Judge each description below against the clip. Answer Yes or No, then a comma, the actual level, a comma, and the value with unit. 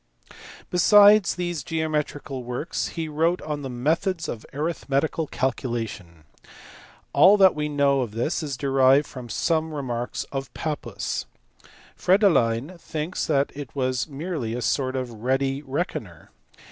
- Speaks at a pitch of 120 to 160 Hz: Yes, medium, 140 Hz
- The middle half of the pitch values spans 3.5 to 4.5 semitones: Yes, average, 3.9 semitones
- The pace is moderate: No, slow, 130 wpm